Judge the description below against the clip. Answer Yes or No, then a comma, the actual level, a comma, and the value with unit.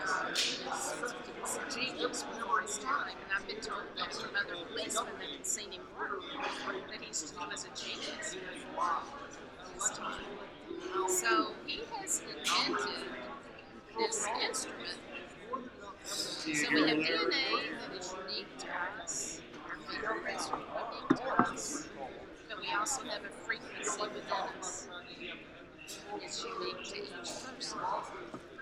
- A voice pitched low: No, very high, 325 Hz